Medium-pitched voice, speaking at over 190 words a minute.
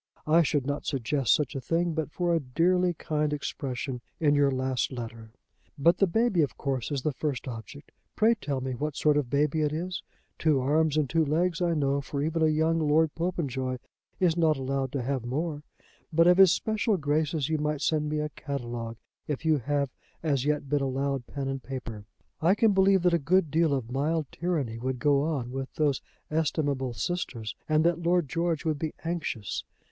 Yes: medium, 150 Hz; average, 200 wpm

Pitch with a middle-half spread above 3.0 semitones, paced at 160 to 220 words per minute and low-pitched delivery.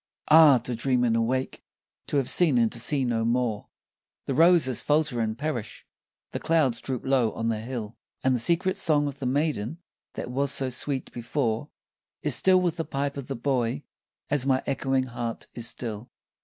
Yes: average, 3.7 semitones; average, 185 wpm; low, 130 Hz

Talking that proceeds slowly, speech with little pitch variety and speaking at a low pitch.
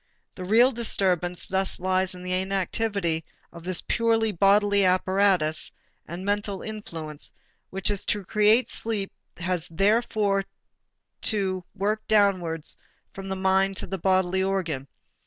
No: slow, 130 wpm; narrow, 2.1 semitones; high, 190 Hz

